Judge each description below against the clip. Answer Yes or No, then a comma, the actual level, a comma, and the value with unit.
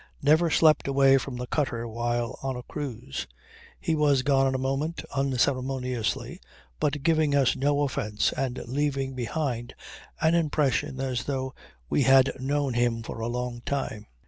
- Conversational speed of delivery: Yes, average, 155 wpm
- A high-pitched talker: No, low, 135 Hz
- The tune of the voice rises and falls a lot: No, average, 2.7 semitones